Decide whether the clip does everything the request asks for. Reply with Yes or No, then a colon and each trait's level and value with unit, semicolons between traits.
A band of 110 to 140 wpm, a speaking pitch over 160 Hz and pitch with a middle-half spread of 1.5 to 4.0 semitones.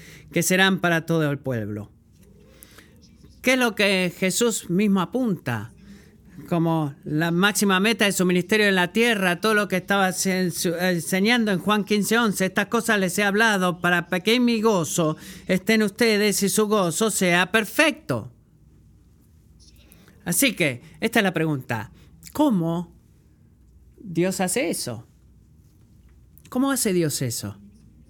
No: average, 135 wpm; medium, 185 Hz; average, 4.4 semitones